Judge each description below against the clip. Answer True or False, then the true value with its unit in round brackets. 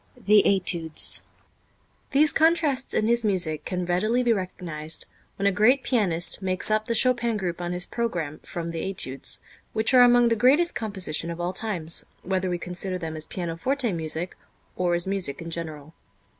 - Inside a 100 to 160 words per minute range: False (170 wpm)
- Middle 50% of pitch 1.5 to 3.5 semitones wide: False (5.4 semitones)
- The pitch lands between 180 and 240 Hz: True (185 Hz)